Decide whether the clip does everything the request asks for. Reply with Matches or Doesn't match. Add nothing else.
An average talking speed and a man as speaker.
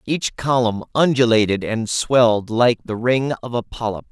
Matches